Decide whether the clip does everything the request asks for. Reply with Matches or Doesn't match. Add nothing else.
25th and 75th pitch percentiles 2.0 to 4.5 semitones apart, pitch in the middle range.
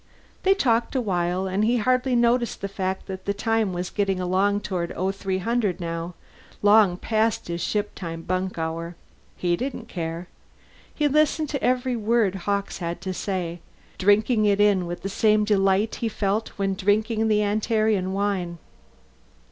Doesn't match